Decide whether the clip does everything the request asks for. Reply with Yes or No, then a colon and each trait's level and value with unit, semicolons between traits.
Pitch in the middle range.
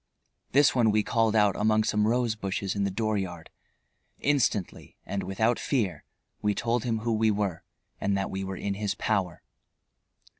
No: low, 105 Hz